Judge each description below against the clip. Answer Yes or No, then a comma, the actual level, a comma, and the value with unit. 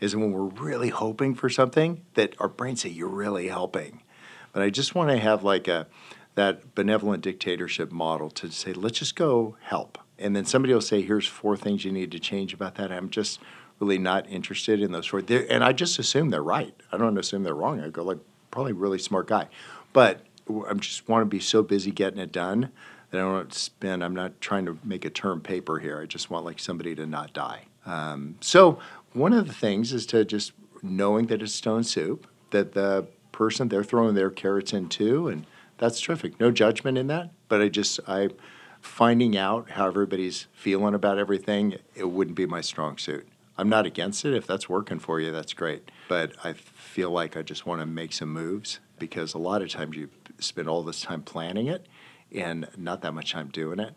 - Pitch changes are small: No, average, 3.3 semitones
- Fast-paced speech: Yes, fast, 220 wpm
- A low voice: Yes, low, 100 Hz